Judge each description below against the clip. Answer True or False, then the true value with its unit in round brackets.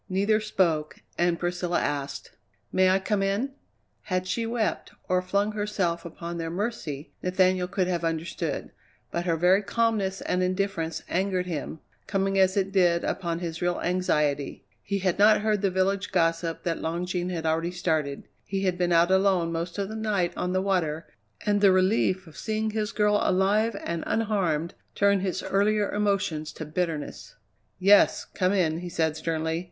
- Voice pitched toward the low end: False (185 Hz)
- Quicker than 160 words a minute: True (170 wpm)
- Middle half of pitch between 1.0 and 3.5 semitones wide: True (2.9 semitones)